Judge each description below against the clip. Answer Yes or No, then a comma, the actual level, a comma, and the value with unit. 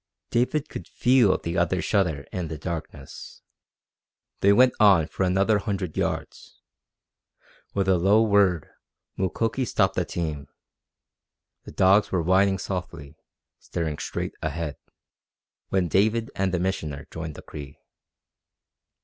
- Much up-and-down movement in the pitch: No, average, 3.8 semitones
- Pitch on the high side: No, very low, 95 Hz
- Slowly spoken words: Yes, slow, 125 wpm